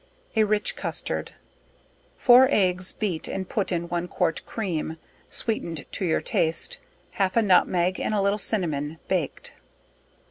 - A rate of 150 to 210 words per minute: No, average, 140 wpm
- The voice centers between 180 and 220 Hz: Yes, medium, 185 Hz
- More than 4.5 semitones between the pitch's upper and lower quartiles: No, average, 3.8 semitones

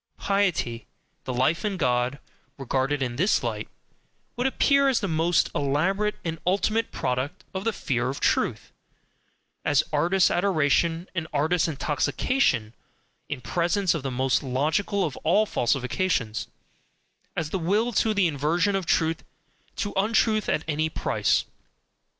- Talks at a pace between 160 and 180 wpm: No, average, 140 wpm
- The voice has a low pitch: No, medium, 165 Hz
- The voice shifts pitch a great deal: Yes, wide, 6.1 semitones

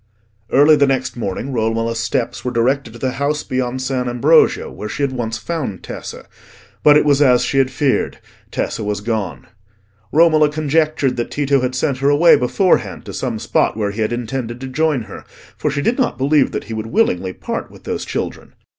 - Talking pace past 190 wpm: Yes, average, 200 wpm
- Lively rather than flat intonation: No, average, 4.1 semitones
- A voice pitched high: No, low, 130 Hz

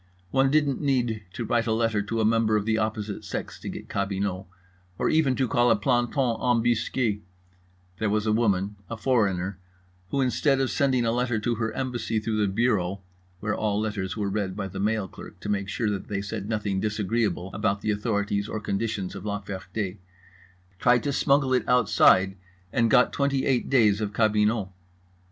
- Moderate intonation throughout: Yes, average, 3.1 semitones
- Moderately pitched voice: No, low, 110 Hz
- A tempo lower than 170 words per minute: No, average, 185 wpm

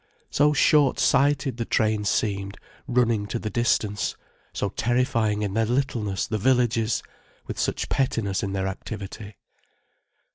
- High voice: No, low, 110 Hz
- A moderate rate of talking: No, slow, 130 wpm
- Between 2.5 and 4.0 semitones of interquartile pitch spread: Yes, average, 3.4 semitones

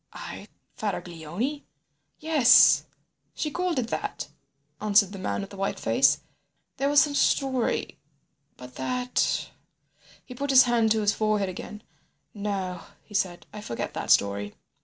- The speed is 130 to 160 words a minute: Yes, slow, 135 wpm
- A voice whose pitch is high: Yes, high, 210 Hz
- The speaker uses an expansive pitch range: Yes, wide, 5.9 semitones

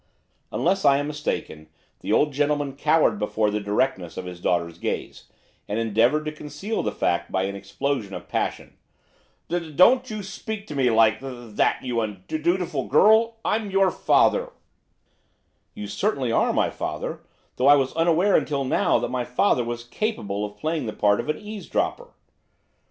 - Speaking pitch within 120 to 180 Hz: Yes, medium, 140 Hz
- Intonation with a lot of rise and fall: Yes, wide, 8.4 semitones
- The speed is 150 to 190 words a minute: Yes, average, 175 wpm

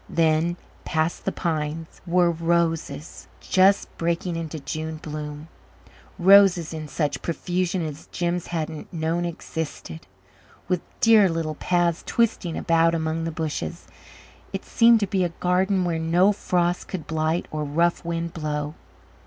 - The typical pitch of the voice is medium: Yes, medium, 165 Hz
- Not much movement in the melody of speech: Yes, narrow, 1.9 semitones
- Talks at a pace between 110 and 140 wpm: Yes, slow, 135 wpm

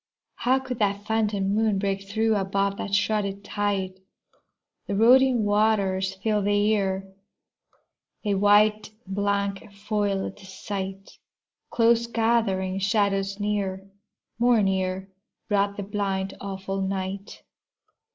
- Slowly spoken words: Yes, slow, 110 wpm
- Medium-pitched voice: No, high, 200 Hz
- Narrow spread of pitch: Yes, narrow, 1.5 semitones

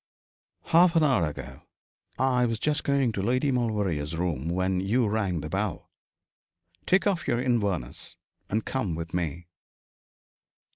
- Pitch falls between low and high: No, low, 105 Hz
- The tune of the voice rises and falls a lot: Yes, wide, 6.6 semitones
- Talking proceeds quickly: No, average, 140 wpm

